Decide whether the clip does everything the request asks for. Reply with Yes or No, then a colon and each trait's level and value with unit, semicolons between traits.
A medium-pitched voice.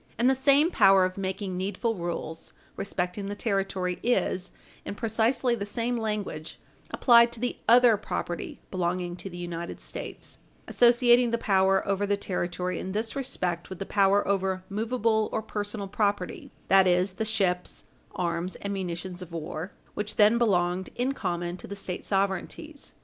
No: high, 195 Hz